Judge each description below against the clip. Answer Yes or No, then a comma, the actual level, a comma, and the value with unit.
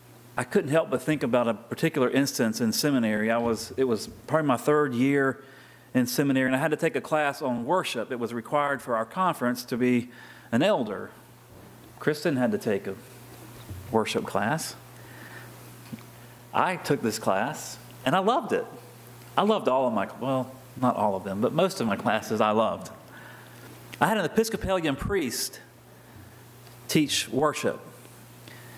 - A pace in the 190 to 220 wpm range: No, average, 165 wpm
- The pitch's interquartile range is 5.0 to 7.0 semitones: No, average, 3.8 semitones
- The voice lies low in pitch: Yes, low, 130 Hz